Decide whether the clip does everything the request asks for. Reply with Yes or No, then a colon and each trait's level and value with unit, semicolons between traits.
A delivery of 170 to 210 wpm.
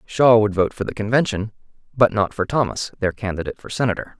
Yes: average, 200 wpm